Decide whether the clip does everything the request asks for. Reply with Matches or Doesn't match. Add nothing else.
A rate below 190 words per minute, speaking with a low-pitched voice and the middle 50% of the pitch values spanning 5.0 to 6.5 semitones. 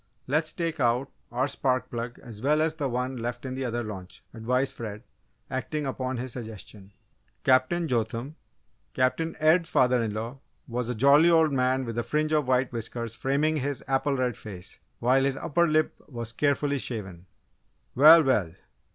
Doesn't match